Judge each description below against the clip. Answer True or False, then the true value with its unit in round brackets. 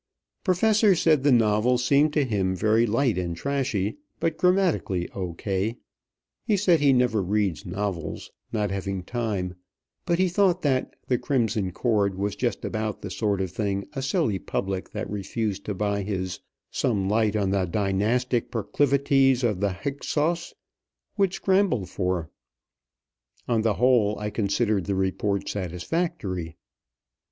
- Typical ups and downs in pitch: False (5.8 semitones)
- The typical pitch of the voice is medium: False (110 Hz)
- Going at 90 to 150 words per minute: True (145 wpm)